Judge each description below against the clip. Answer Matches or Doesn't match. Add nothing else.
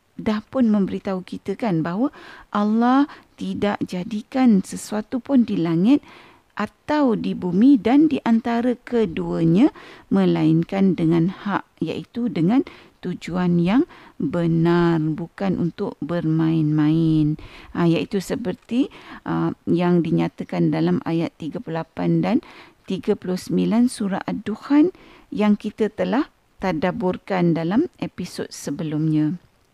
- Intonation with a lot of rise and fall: Matches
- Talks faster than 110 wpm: Doesn't match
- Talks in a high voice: Matches